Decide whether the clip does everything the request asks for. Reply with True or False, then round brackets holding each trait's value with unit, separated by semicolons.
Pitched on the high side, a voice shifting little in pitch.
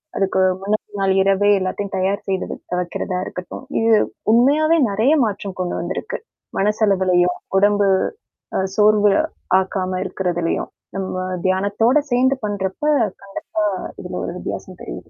True (195 Hz; 2.3 semitones)